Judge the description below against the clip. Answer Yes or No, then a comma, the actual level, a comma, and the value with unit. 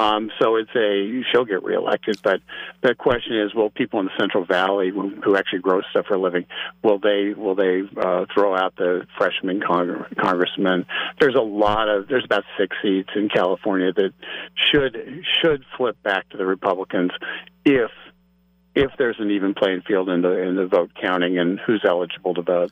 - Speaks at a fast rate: No, average, 190 wpm